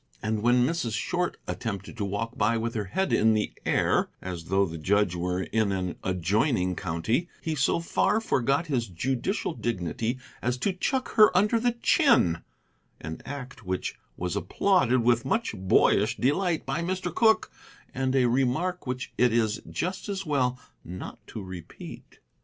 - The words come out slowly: No, average, 165 wpm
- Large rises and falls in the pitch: Yes, wide, 8.6 semitones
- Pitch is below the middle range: Yes, low, 120 Hz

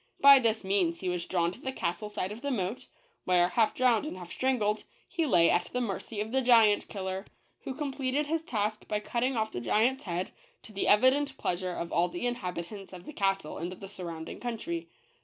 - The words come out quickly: Yes, fast, 215 wpm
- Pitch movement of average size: No, wide, 5.9 semitones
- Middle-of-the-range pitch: No, high, 210 Hz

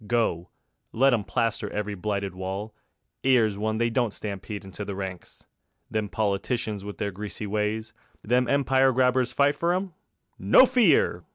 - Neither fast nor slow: Yes, average, 155 wpm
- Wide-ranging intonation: No, average, 4.0 semitones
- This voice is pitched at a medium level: No, low, 110 Hz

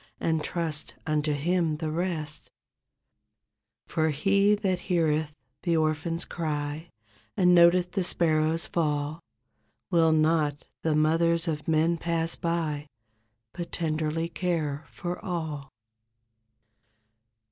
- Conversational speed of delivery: No, slow, 110 wpm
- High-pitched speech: No, medium, 160 Hz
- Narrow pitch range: Yes, narrow, 1.9 semitones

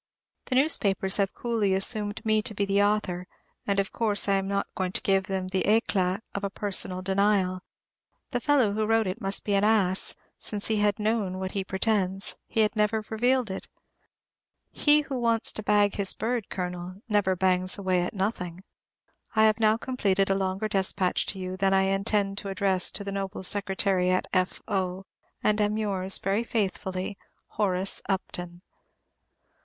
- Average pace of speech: Yes, average, 180 wpm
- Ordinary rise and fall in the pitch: No, narrow, 2.1 semitones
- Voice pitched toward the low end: No, high, 200 Hz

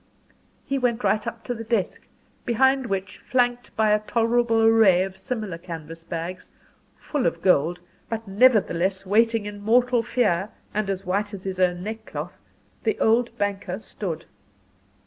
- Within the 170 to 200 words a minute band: No, average, 155 wpm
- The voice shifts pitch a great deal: No, average, 3.8 semitones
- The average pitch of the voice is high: Yes, high, 210 Hz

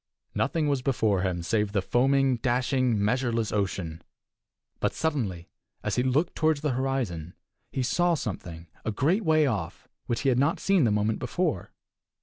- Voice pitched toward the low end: Yes, low, 125 Hz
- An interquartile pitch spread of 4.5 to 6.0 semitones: Yes, average, 5.2 semitones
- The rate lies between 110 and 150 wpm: No, average, 160 wpm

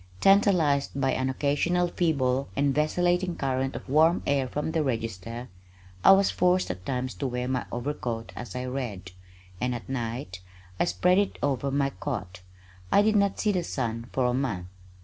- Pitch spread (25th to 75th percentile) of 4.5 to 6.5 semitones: Yes, average, 5.1 semitones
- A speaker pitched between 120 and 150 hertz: Yes, low, 135 Hz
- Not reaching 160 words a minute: No, average, 175 wpm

